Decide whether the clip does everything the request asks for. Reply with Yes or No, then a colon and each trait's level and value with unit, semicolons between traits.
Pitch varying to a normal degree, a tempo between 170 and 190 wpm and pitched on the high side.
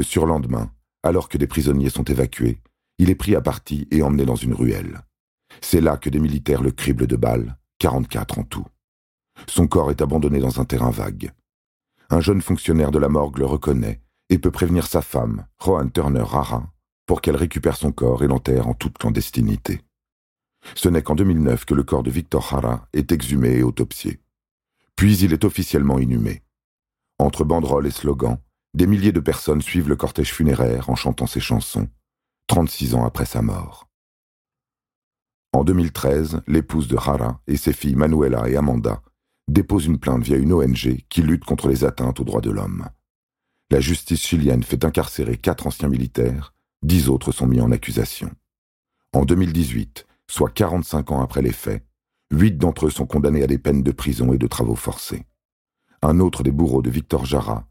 No: average, 3.6 semitones; average, 180 wpm; very low, 70 Hz